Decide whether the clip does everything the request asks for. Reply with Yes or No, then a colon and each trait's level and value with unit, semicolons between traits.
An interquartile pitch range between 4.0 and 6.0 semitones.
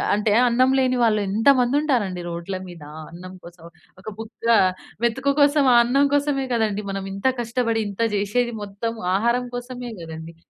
Yes: average, 4.3 semitones